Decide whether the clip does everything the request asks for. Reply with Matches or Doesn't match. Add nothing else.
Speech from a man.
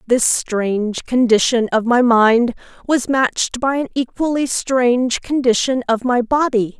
Doesn't match